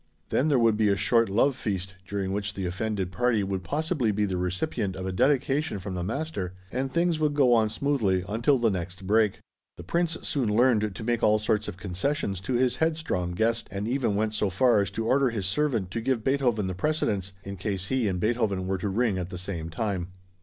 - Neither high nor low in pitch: No, low, 105 Hz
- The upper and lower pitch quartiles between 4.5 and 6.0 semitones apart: Yes, average, 4.8 semitones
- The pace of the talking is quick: Yes, fast, 220 wpm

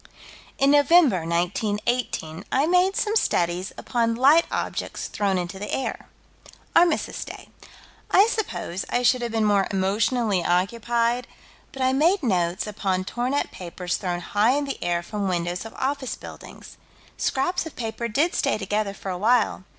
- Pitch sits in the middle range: No, high, 225 Hz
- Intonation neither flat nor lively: No, wide, 6.2 semitones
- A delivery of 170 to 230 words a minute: No, average, 160 wpm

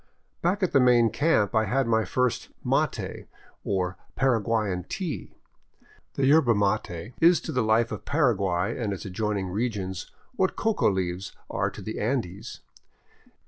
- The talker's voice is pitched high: No, low, 110 Hz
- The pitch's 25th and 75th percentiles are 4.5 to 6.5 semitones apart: Yes, wide, 5.4 semitones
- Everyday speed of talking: Yes, average, 150 wpm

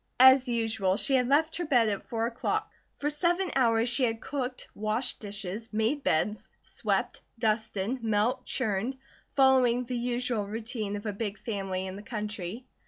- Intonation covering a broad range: No, average, 3.5 semitones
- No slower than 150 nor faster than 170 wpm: Yes, average, 165 wpm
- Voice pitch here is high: Yes, high, 230 Hz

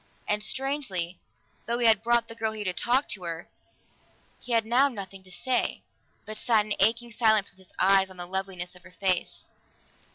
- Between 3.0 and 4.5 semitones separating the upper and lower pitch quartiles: Yes, average, 3.9 semitones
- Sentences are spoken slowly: No, average, 195 wpm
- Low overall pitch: No, high, 210 Hz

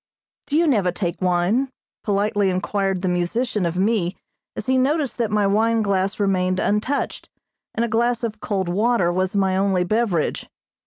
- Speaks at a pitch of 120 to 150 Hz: No, high, 200 Hz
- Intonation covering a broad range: No, average, 3.7 semitones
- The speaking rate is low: No, average, 165 wpm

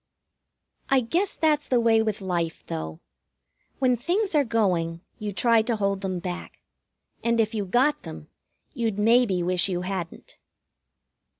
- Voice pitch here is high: Yes, high, 215 Hz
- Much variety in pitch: No, average, 4.9 semitones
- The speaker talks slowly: No, average, 145 wpm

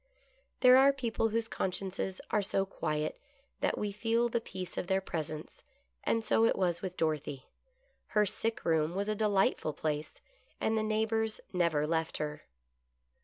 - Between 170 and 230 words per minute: No, average, 160 wpm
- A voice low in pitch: No, high, 195 Hz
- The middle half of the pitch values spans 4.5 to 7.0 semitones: Yes, wide, 5.4 semitones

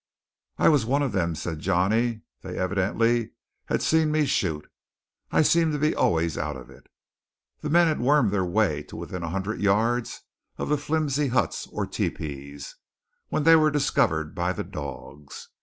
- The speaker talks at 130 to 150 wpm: No, average, 175 wpm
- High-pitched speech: No, low, 110 Hz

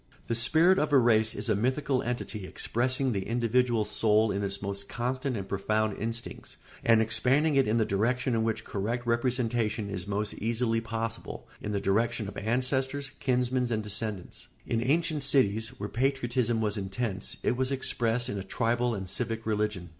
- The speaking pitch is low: Yes, low, 115 Hz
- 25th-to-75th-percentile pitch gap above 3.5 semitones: No, average, 2.9 semitones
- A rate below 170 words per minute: No, average, 175 wpm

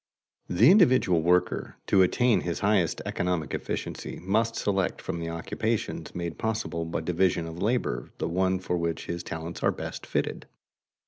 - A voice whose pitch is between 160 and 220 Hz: No, very low, 90 Hz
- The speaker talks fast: No, average, 155 wpm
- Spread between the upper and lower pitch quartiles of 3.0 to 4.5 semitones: Yes, average, 3.8 semitones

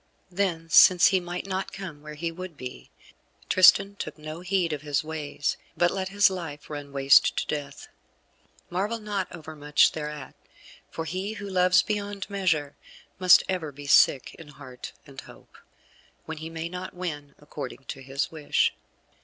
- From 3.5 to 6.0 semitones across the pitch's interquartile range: Yes, average, 4.1 semitones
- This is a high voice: No, medium, 165 Hz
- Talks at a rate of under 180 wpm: Yes, average, 160 wpm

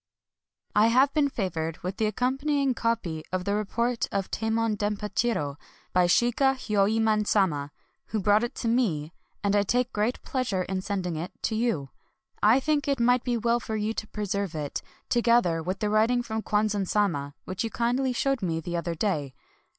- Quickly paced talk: No, average, 190 wpm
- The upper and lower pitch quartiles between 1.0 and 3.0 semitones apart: No, average, 4.4 semitones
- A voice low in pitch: No, high, 215 Hz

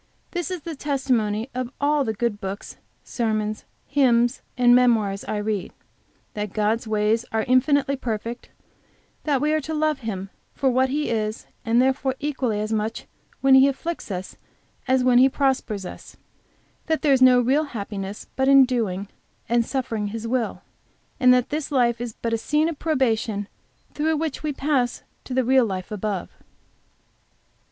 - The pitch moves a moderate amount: Yes, average, 4.1 semitones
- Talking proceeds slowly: No, average, 165 wpm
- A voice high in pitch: Yes, high, 245 Hz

